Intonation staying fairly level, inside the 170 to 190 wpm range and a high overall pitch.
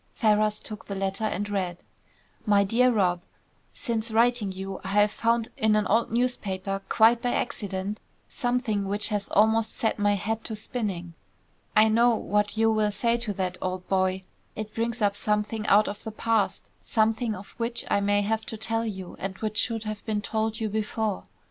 Yes: narrow, 2.0 semitones; average, 185 wpm; high, 215 Hz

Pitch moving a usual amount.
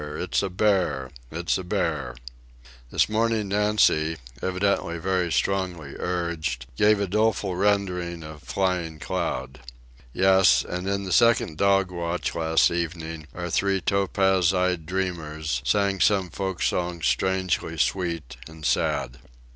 Yes: average, 3.2 semitones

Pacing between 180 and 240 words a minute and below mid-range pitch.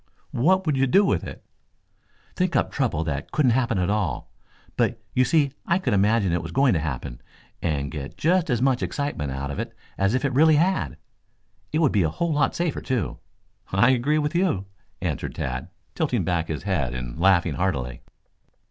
Yes: average, 190 wpm; low, 115 Hz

